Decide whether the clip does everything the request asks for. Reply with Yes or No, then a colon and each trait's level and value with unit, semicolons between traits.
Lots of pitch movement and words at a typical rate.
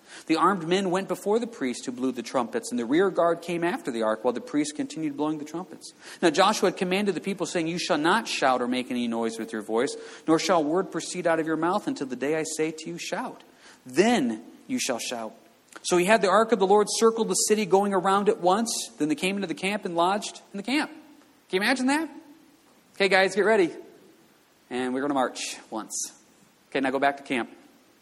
No: wide, 7.5 semitones; fast, 235 wpm